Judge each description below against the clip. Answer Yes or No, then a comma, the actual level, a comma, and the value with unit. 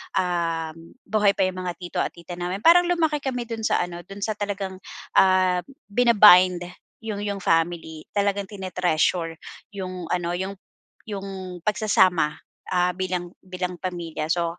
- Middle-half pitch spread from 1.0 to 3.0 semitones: Yes, narrow, 2.4 semitones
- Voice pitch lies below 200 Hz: Yes, medium, 185 Hz